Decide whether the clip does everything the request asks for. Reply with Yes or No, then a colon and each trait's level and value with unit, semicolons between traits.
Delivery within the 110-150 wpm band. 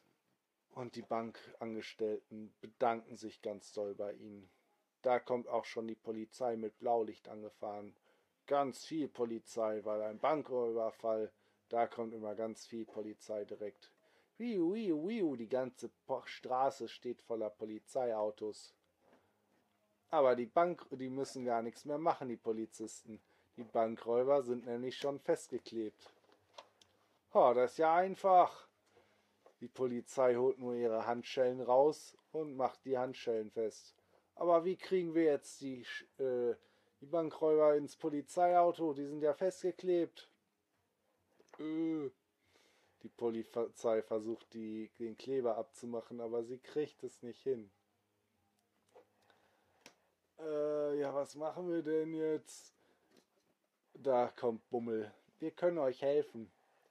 Yes: slow, 125 wpm